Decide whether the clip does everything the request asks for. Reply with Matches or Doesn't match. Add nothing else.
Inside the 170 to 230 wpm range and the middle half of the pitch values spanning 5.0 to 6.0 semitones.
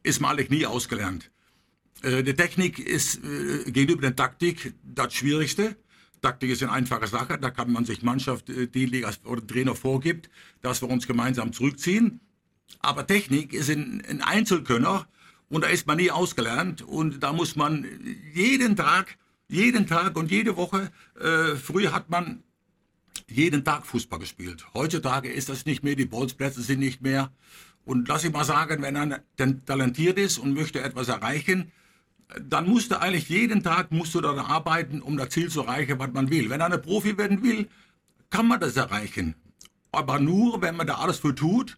Matches